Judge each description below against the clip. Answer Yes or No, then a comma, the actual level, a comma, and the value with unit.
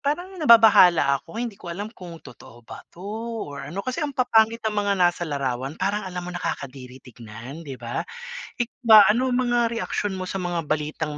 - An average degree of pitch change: No, wide, 7.9 semitones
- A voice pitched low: No, medium, 180 Hz